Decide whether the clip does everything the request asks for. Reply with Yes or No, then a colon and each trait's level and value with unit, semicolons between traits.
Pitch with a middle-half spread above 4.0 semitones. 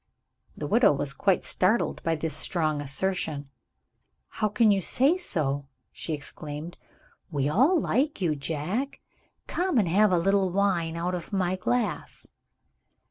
Yes: wide, 5.6 semitones